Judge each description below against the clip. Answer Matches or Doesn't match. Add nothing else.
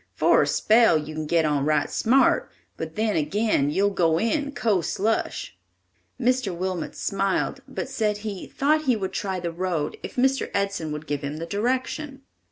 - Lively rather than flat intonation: Matches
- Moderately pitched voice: Doesn't match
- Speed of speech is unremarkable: Matches